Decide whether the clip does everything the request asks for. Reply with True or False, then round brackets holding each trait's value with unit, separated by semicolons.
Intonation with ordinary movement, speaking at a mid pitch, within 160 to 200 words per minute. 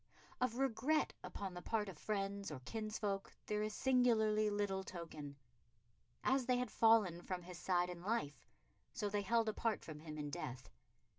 False (4.2 semitones; 205 Hz; 165 wpm)